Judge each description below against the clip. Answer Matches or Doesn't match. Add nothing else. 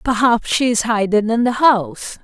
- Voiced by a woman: Matches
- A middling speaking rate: Matches